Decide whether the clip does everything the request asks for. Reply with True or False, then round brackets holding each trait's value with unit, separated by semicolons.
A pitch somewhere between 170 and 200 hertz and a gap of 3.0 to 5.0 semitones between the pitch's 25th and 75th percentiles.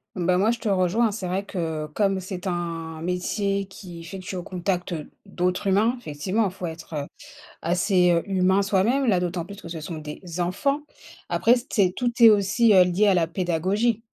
False (185 Hz; 2.6 semitones)